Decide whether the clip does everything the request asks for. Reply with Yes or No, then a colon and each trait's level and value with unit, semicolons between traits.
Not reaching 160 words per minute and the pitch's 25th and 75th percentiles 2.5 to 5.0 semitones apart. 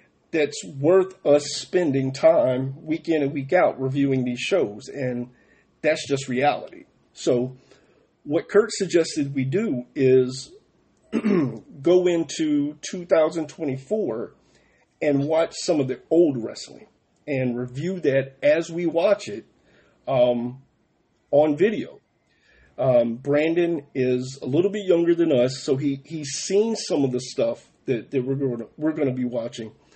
Yes: average, 140 wpm; average, 4.2 semitones